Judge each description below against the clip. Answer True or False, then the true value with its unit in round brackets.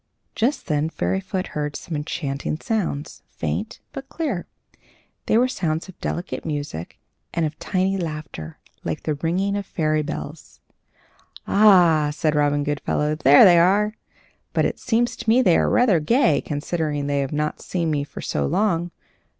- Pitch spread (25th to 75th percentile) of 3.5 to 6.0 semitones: True (4.6 semitones)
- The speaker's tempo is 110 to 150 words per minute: False (160 wpm)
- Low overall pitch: False (160 Hz)